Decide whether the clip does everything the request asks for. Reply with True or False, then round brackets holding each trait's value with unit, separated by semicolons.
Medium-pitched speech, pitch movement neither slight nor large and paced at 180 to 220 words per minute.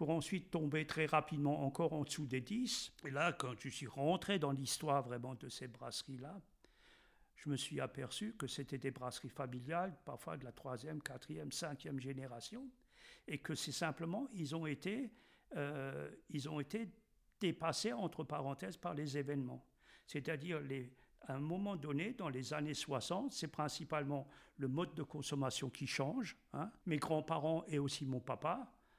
False (150 Hz; 3.6 semitones; 165 wpm)